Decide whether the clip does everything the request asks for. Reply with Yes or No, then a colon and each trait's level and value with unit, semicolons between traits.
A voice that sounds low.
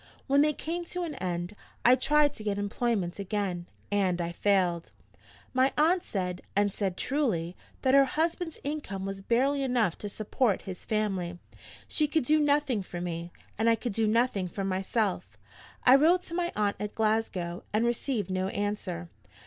No: high, 215 Hz